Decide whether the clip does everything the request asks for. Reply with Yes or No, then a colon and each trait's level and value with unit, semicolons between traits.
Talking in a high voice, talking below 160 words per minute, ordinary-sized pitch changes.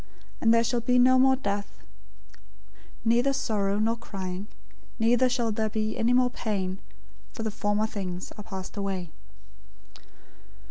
Yes: high, 220 Hz; average, 140 wpm; average, 3.3 semitones